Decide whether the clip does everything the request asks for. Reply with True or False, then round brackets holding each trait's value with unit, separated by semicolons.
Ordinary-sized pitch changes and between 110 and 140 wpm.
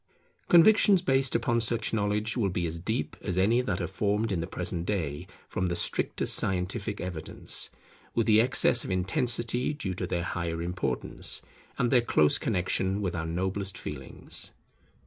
False (4.8 semitones; 165 wpm)